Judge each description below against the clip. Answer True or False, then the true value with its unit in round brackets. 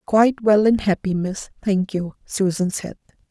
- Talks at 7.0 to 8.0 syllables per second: False (4.5 syllables/s)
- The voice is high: True (200 Hz)